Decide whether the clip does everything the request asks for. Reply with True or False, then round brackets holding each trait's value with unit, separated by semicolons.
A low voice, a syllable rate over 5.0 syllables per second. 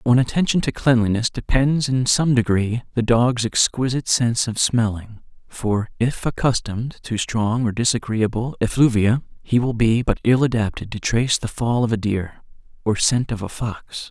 False (115 Hz; 4.9 syllables/s)